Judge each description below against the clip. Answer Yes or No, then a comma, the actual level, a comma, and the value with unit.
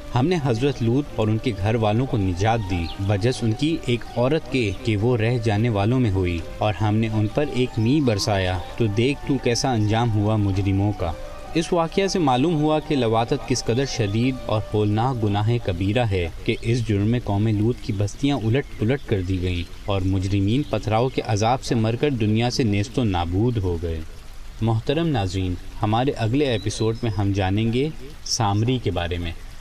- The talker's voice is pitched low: Yes, low, 110 Hz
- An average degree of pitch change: Yes, average, 4.0 semitones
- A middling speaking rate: No, fast, 195 wpm